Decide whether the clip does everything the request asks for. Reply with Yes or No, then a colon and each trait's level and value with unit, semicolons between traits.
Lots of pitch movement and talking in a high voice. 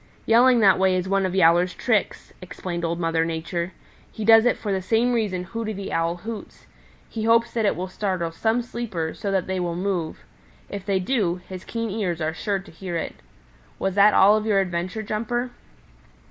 No: average, 3.8 semitones; high, 195 Hz